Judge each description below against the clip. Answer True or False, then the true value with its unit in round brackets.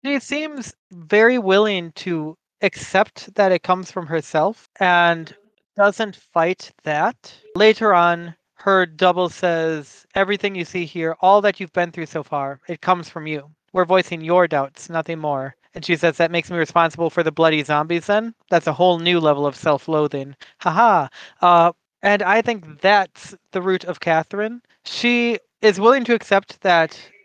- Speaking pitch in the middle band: True (175 Hz)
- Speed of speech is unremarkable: True (170 wpm)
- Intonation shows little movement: False (3.6 semitones)